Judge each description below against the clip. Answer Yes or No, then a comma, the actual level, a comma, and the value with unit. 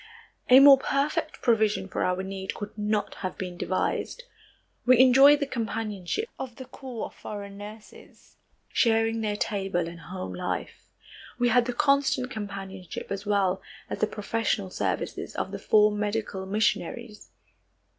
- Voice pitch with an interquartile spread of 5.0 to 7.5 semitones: No, average, 4.1 semitones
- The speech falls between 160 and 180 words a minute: No, average, 145 wpm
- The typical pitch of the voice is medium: No, high, 210 Hz